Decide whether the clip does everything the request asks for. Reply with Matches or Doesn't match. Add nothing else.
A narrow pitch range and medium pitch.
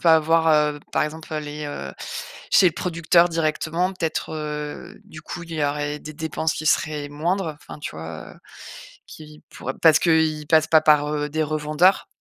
Matches